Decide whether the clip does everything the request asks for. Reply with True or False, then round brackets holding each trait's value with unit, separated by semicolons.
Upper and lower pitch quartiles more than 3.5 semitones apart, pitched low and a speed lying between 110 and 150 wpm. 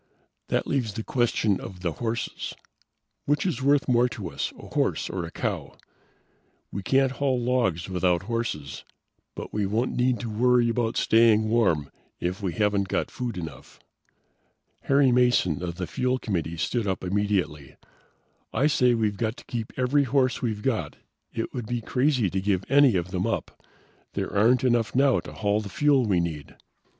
False (4.9 semitones; 110 Hz; 175 wpm)